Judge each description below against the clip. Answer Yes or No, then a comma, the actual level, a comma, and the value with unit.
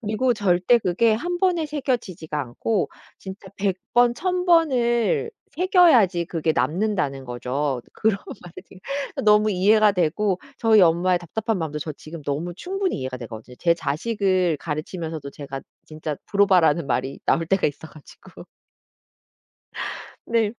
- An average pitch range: No, wide, 6.8 semitones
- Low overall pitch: No, medium, 185 Hz